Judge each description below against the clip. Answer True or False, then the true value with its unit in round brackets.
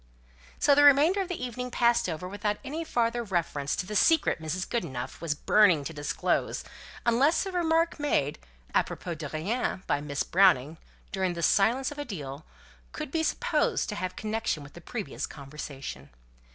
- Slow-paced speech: False (170 wpm)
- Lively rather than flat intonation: True (8.7 semitones)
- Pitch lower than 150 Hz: False (200 Hz)